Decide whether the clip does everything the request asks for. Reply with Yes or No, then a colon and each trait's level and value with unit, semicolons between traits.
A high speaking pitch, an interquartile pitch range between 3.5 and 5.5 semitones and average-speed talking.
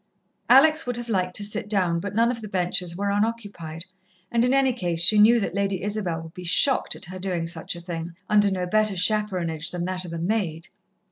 No: high, 195 Hz; average, 3.8 semitones; fast, 220 wpm